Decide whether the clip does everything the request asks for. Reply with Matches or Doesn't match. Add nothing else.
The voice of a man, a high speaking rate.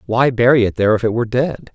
Matches